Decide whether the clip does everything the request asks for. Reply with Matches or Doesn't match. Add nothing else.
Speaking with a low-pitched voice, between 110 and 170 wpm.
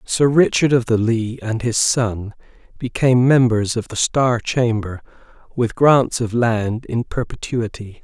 Matches